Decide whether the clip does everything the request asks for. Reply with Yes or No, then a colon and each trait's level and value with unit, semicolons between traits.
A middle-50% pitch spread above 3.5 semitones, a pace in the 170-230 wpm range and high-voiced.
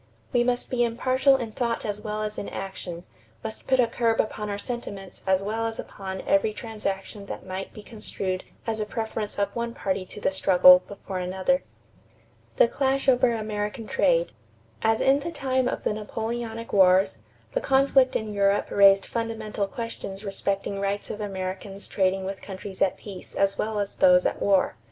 No: average, 3.2 semitones; average, 180 wpm; high, 210 Hz